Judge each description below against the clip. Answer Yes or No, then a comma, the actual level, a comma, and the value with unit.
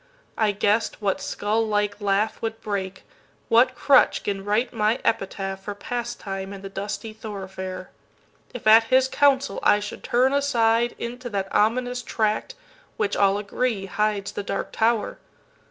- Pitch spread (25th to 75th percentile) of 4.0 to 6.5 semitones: No, average, 3.0 semitones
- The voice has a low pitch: No, high, 215 Hz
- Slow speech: Yes, slow, 130 wpm